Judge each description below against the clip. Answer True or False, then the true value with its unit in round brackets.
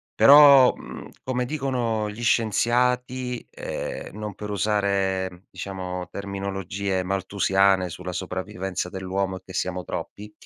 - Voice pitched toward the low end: True (100 Hz)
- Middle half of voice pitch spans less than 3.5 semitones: False (3.8 semitones)